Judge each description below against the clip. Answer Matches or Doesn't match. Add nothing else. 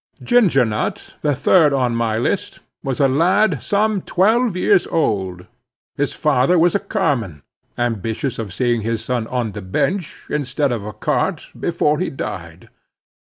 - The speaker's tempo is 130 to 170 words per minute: Matches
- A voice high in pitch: Doesn't match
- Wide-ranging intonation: Matches